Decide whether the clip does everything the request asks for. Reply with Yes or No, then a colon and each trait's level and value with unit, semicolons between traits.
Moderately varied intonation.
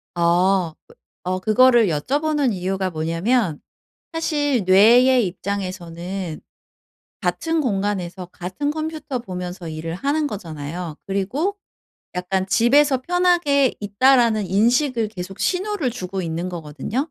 No: wide, 6.9 semitones